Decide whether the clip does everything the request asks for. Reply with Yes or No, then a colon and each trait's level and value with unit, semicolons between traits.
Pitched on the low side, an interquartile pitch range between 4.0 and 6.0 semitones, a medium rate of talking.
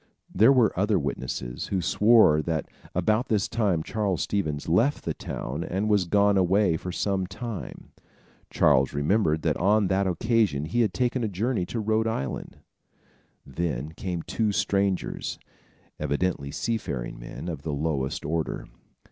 Yes: very low, 95 Hz; wide, 5.5 semitones; average, 150 wpm